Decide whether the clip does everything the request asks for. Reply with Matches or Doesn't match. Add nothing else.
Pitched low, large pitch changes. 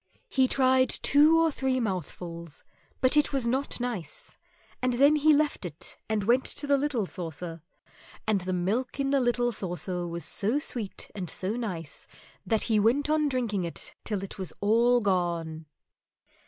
Doesn't match